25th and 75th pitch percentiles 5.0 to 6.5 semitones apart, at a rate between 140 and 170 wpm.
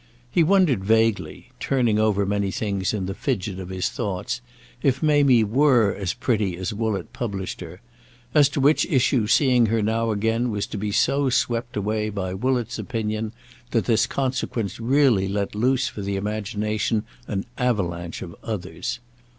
No: average, 3.8 semitones; average, 160 wpm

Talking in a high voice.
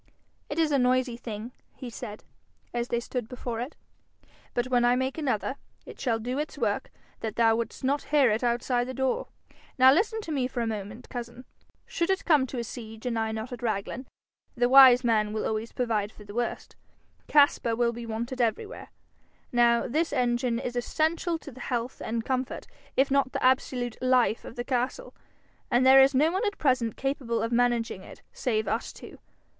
Yes: high, 245 Hz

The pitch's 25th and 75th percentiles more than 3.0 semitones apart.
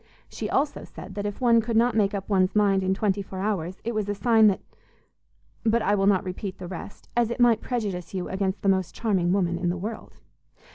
No: average, 2.7 semitones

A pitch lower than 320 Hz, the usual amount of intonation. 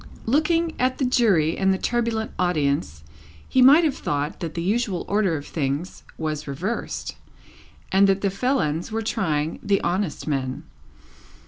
No: high, 190 Hz; wide, 7.2 semitones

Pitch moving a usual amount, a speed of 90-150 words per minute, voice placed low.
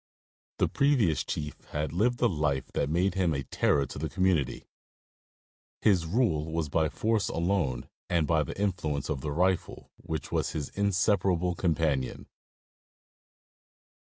Yes: average, 4.3 semitones; average, 140 wpm; very low, 80 Hz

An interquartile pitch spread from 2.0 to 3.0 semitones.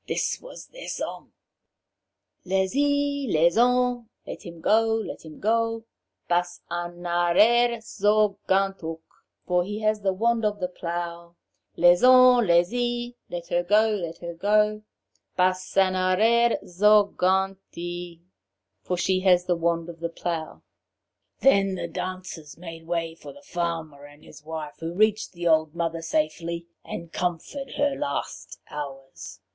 No: average, 4.2 semitones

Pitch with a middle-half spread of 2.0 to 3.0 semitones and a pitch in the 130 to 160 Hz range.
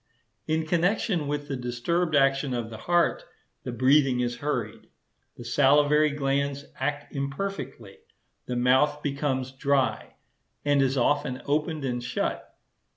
Yes: narrow, 2.5 semitones; medium, 140 Hz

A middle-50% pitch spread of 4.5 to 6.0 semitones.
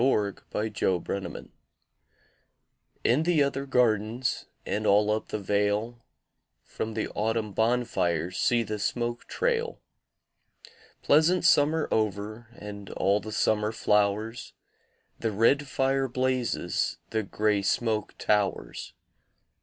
No: average, 3.5 semitones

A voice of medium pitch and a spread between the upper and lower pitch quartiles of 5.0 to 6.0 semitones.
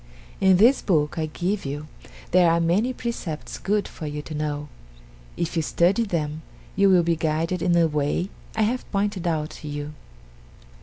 No: medium, 170 Hz; average, 4.2 semitones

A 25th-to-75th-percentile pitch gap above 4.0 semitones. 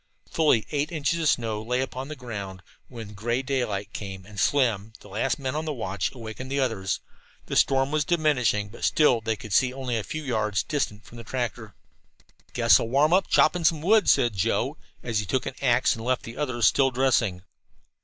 Yes: average, 4.4 semitones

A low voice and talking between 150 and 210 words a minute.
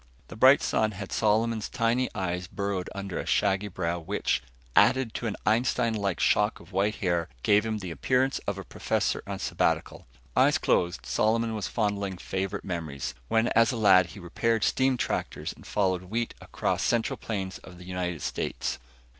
Yes: low, 100 Hz; average, 175 wpm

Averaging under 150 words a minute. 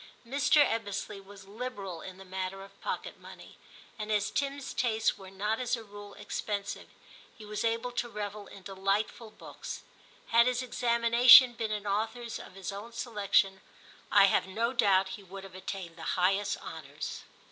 No: average, 170 wpm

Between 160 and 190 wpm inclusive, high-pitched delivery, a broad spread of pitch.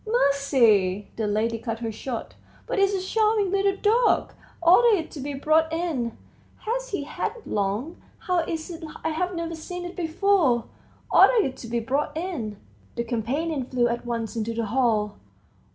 Yes: average, 170 wpm; very high, 290 Hz; wide, 7.6 semitones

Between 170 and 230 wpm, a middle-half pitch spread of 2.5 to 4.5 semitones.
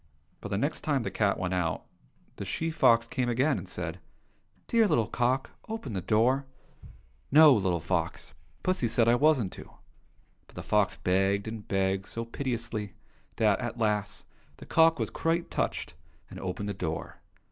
No: average, 180 wpm; wide, 5.4 semitones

